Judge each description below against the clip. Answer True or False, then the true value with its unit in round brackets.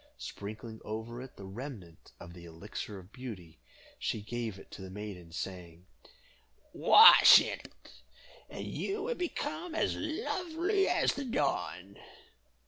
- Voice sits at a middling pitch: False (110 Hz)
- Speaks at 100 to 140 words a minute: True (135 wpm)